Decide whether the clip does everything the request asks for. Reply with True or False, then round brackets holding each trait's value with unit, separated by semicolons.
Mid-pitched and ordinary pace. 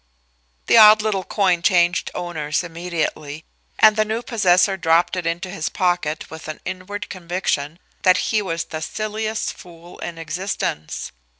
True (180 Hz; 145 wpm)